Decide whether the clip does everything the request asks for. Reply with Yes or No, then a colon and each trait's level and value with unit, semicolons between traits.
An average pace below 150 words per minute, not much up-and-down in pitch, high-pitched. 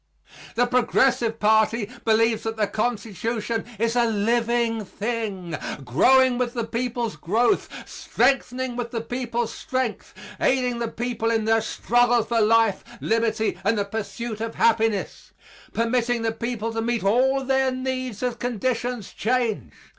Yes: average, 140 wpm; narrow, 1.7 semitones; high, 230 Hz